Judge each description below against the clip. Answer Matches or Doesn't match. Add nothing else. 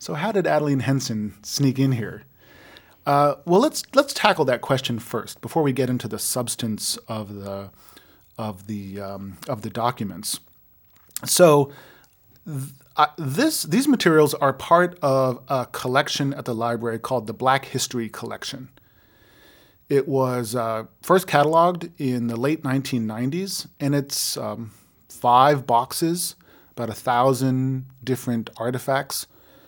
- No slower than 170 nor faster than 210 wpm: Doesn't match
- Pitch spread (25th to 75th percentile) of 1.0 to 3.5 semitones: Doesn't match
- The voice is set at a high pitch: Doesn't match